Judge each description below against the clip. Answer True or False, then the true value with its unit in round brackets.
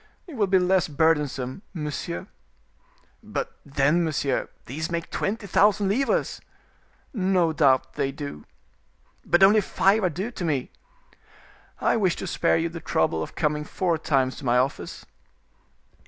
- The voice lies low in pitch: False (165 Hz)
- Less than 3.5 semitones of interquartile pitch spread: False (5.3 semitones)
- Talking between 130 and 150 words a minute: True (145 wpm)